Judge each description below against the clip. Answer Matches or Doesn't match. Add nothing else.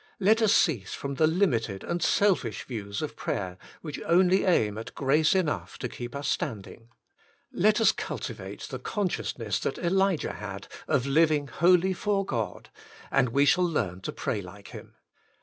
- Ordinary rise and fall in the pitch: Doesn't match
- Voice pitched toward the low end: Doesn't match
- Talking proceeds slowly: Doesn't match